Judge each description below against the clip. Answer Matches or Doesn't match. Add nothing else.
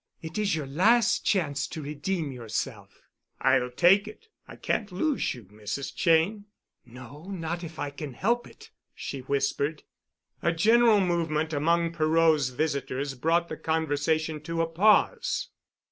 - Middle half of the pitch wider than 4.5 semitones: Doesn't match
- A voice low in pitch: Doesn't match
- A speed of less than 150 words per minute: Matches